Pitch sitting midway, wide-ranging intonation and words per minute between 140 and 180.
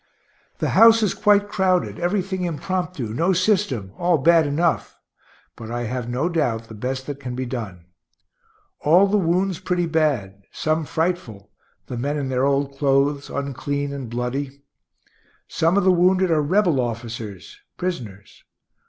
Yes: medium, 145 Hz; wide, 6.3 semitones; average, 150 wpm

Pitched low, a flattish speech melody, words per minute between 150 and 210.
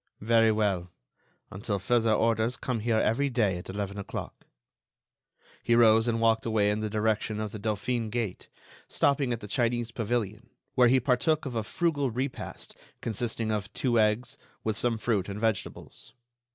Yes: low, 110 Hz; narrow, 2.3 semitones; average, 165 wpm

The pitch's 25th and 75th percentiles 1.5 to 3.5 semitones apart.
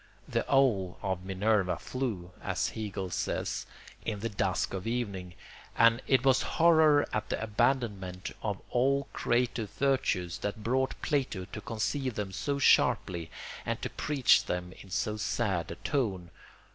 No: wide, 5.6 semitones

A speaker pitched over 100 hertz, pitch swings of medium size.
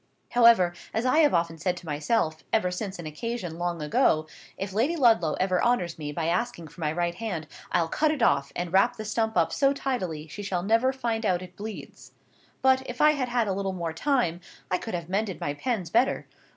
No: high, 190 Hz; wide, 5.8 semitones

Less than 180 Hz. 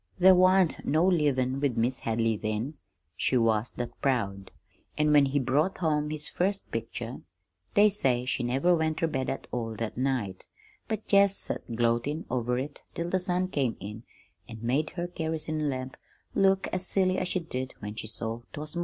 Yes: medium, 140 Hz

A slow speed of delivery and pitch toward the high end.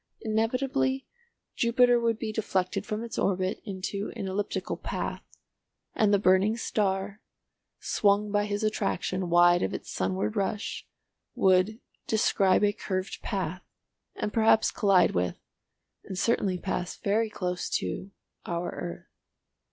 Yes: slow, 130 wpm; high, 200 Hz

